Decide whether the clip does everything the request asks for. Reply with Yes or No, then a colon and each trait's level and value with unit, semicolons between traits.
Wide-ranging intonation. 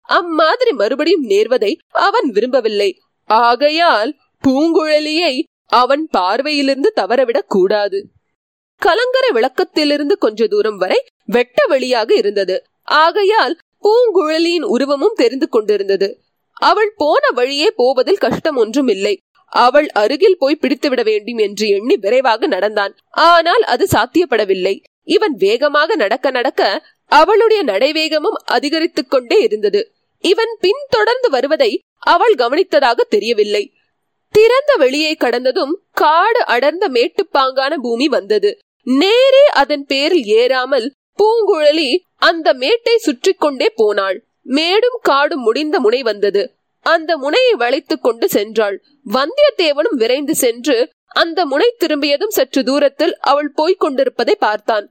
Yes: wide, 7.0 semitones